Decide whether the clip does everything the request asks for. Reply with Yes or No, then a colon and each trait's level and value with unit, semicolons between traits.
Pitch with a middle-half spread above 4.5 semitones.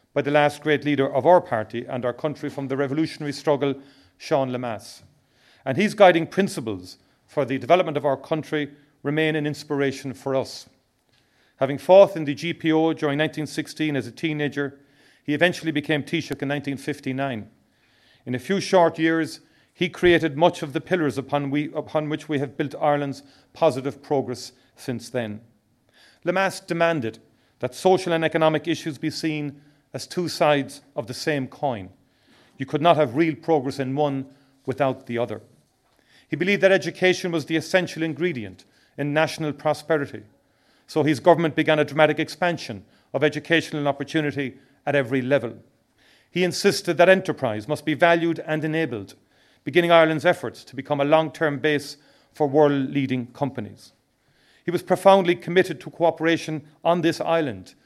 No: average, 3.2 semitones